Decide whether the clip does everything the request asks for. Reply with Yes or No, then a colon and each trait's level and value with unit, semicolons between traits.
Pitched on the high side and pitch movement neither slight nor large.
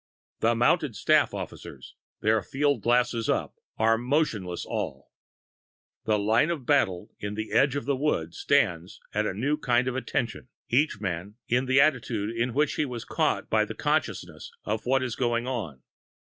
No: low, 120 Hz; average, 3.9 semitones